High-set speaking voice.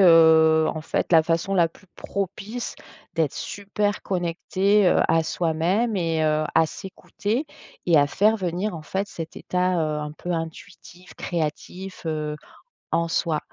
No: medium, 170 Hz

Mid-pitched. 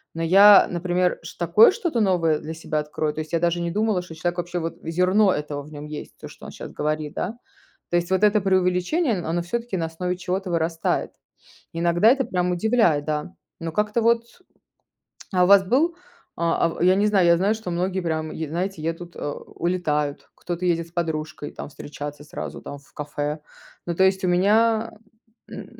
Yes: medium, 175 Hz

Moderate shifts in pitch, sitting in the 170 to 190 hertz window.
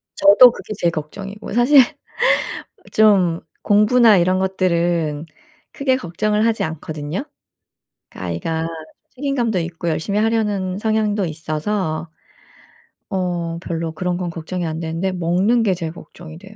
Yes: average, 4.2 semitones; medium, 185 Hz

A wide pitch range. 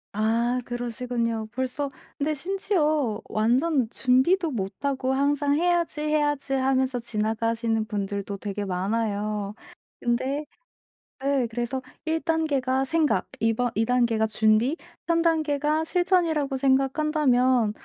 No: average, 4.8 semitones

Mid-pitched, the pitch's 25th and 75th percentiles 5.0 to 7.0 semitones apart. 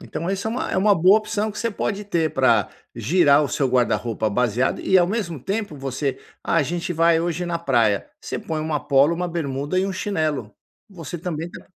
Yes: medium, 165 Hz; wide, 5.4 semitones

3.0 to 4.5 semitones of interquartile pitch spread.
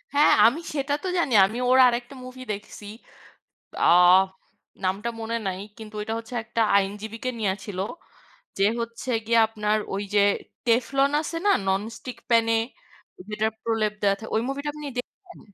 Yes: average, 3.4 semitones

